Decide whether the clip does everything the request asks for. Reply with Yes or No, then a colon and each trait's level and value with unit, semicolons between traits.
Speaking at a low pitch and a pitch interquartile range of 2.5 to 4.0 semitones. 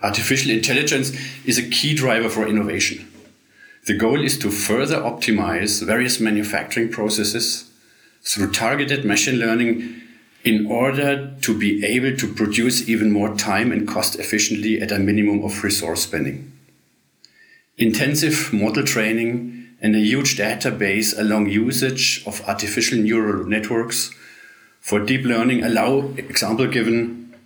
Yes: low, 115 Hz; average, 2.9 semitones